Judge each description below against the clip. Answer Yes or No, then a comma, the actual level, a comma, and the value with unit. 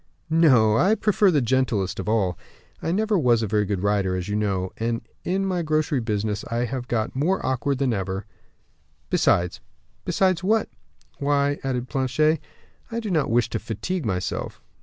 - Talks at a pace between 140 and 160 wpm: No, average, 175 wpm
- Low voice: Yes, low, 125 Hz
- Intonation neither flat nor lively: No, wide, 7.1 semitones